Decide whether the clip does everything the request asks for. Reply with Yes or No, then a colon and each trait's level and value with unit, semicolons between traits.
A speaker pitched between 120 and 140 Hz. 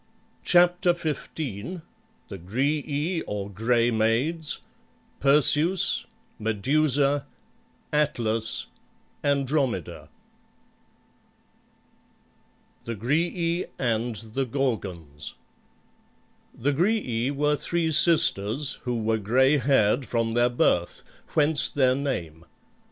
Yes: low, 135 Hz